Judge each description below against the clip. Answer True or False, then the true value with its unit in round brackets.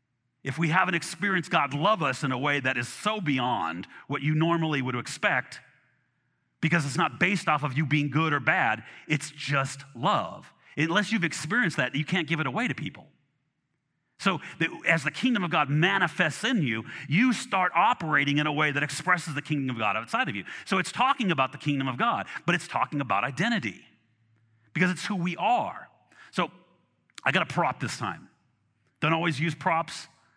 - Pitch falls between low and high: True (155 Hz)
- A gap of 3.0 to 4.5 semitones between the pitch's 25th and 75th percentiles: True (3.9 semitones)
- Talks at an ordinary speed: True (190 wpm)